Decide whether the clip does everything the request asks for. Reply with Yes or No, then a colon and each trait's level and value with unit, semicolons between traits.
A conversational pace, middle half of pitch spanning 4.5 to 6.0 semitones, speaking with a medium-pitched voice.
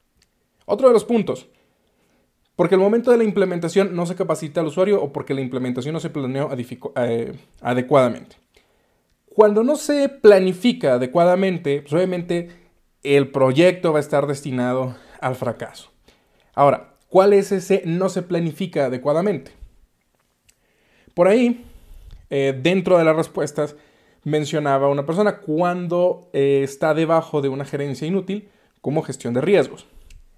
Yes: average, 140 wpm; wide, 5.5 semitones; medium, 160 Hz